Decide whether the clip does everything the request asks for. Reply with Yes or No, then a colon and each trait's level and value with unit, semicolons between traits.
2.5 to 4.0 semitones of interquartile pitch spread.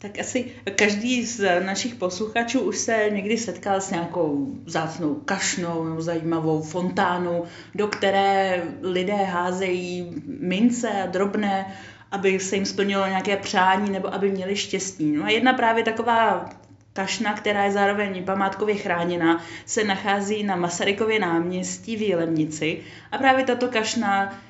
Yes: average, 2.8 semitones